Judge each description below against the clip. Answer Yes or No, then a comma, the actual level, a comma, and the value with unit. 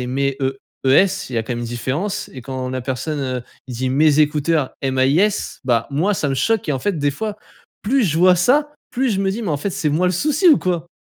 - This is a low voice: No, medium, 150 Hz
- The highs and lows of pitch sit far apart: Yes, wide, 6.9 semitones